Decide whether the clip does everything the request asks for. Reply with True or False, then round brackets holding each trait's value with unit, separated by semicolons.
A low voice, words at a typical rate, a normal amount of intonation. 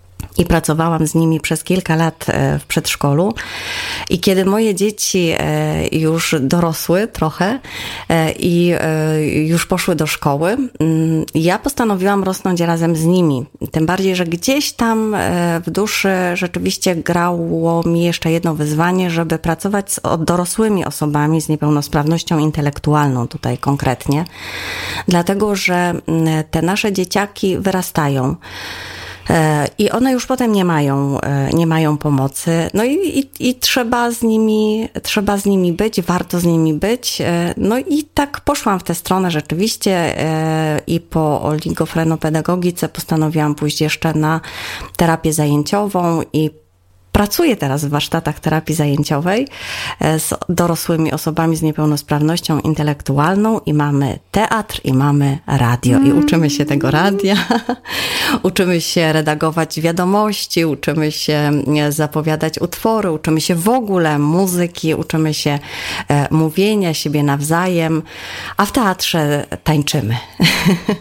False (165 Hz; 120 wpm; 3.7 semitones)